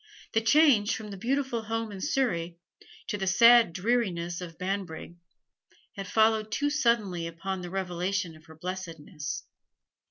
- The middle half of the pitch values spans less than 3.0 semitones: No, average, 4.6 semitones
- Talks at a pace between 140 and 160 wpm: Yes, average, 145 wpm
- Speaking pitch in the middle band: No, high, 195 Hz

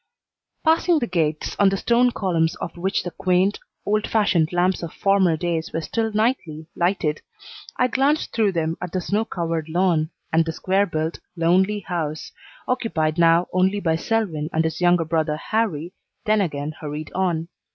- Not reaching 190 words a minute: Yes, average, 170 wpm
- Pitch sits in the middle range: Yes, medium, 175 Hz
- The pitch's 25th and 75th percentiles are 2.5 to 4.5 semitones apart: Yes, average, 4.0 semitones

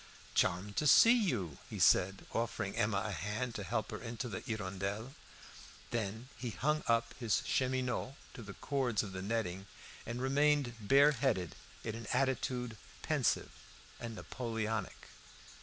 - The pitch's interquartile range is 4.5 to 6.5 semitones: No, average, 3.9 semitones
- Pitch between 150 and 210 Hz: No, low, 115 Hz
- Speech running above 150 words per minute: No, average, 145 wpm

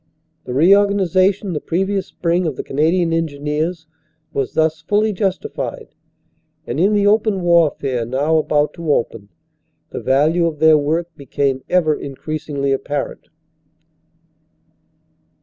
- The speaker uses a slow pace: Yes, slow, 125 wpm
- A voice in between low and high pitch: Yes, medium, 160 Hz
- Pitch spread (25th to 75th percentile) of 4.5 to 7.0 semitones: No, average, 4.1 semitones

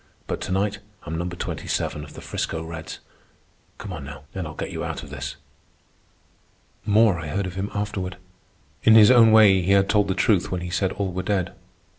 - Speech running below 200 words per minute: No, fast, 205 wpm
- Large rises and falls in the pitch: No, average, 2.8 semitones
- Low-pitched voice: Yes, very low, 95 Hz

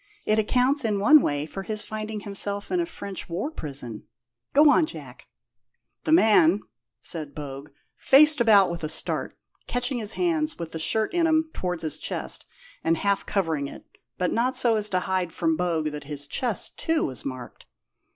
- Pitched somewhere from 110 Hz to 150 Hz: No, high, 200 Hz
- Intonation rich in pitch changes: Yes, wide, 7.6 semitones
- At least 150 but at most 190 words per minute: Yes, average, 180 wpm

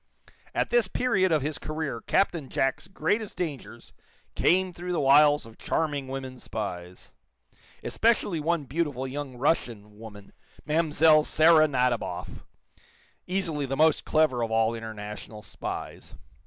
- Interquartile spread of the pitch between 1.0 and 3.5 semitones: No, wide, 5.4 semitones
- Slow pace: Yes, slow, 130 wpm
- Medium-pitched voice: Yes, medium, 145 Hz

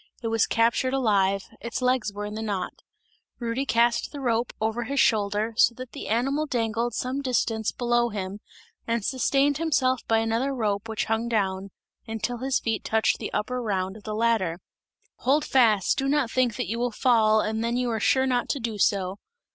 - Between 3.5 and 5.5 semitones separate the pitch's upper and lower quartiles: No, average, 2.9 semitones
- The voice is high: Yes, high, 230 Hz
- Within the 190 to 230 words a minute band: Yes, average, 195 wpm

